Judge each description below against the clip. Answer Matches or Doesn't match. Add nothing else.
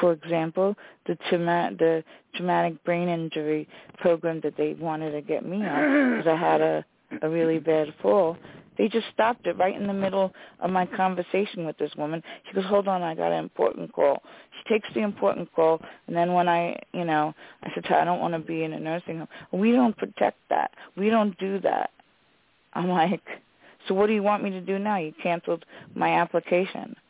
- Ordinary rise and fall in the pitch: Matches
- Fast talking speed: Matches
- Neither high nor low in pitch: Matches